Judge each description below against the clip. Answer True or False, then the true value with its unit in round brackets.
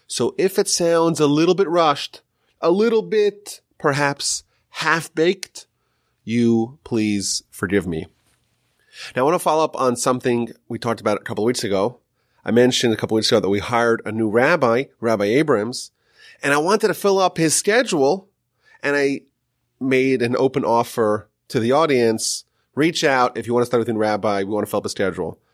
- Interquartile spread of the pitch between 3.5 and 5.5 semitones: True (4.8 semitones)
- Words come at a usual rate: True (195 wpm)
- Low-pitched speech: True (120 Hz)